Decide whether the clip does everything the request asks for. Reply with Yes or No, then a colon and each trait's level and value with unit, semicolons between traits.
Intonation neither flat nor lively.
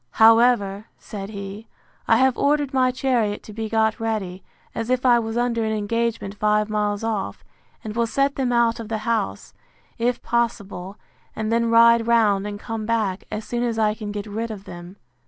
No: narrow, 2.2 semitones